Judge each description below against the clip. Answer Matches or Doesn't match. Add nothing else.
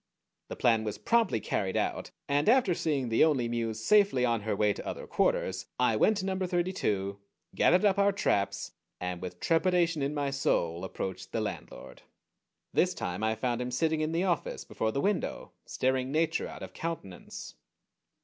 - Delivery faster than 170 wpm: Matches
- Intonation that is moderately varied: Doesn't match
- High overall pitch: Doesn't match